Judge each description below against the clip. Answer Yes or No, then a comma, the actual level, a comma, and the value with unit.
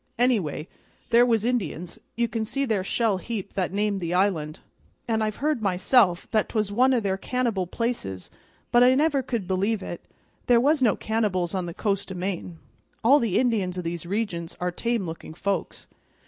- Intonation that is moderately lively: Yes, average, 4.6 semitones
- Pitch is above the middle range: Yes, high, 205 Hz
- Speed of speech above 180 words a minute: Yes, average, 190 wpm